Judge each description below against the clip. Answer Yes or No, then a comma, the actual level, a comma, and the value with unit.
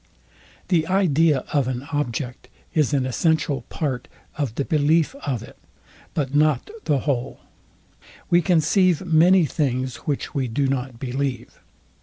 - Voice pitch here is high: No, medium, 145 Hz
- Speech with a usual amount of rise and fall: Yes, average, 3.6 semitones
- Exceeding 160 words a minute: No, slow, 135 wpm